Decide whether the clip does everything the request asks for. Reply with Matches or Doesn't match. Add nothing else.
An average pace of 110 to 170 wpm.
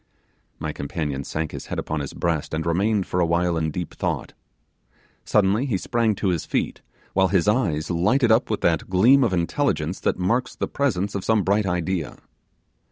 Doesn't match